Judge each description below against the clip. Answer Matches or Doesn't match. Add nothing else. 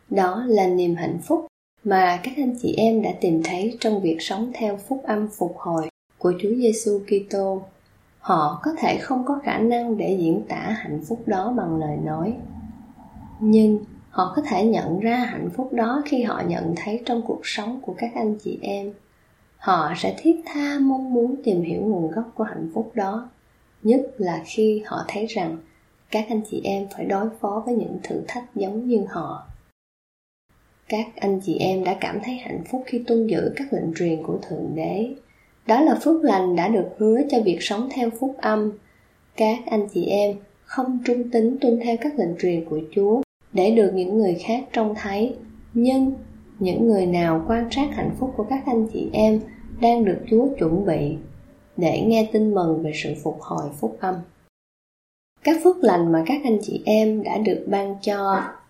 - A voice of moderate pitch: Doesn't match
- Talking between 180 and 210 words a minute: Matches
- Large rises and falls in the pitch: Doesn't match